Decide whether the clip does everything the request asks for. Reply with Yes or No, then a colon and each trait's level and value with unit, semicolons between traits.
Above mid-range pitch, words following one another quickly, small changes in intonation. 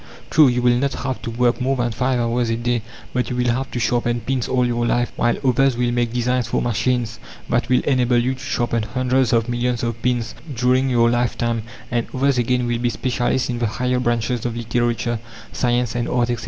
No: low, 120 Hz; fast, 220 wpm; narrow, 1.1 semitones